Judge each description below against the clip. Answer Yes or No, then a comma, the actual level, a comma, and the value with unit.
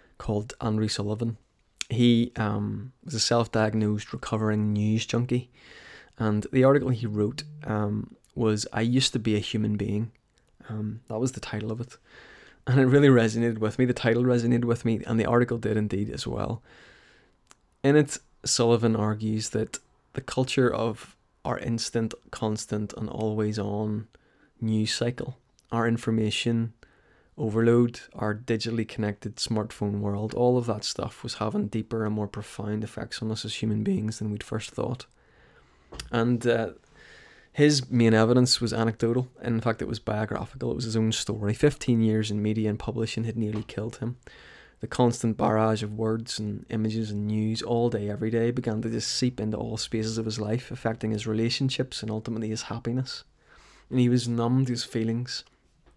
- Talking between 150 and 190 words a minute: Yes, average, 170 wpm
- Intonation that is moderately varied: No, narrow, 1.8 semitones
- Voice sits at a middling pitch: No, low, 115 Hz